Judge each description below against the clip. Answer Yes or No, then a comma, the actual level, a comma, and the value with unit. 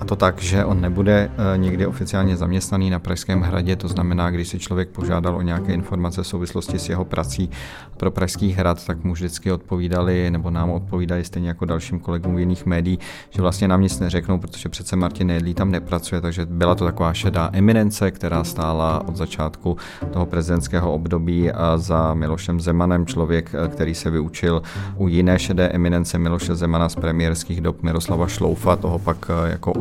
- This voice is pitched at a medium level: No, very low, 90 Hz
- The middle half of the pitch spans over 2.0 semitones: No, narrow, 1.5 semitones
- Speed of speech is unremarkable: No, fast, 175 wpm